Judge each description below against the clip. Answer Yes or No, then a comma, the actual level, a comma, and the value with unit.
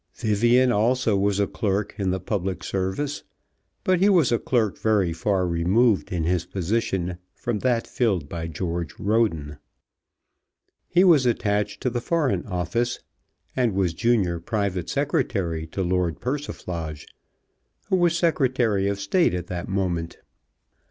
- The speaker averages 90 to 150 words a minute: Yes, average, 140 wpm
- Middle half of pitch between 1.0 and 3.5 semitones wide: No, average, 5.3 semitones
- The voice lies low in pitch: Yes, low, 100 Hz